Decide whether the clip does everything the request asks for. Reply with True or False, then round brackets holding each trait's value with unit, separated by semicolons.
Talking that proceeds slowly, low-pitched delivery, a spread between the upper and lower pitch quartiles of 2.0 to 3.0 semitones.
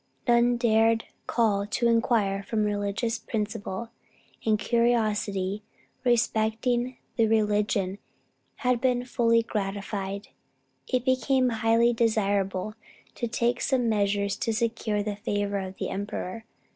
False (115 wpm; 220 Hz; 2.6 semitones)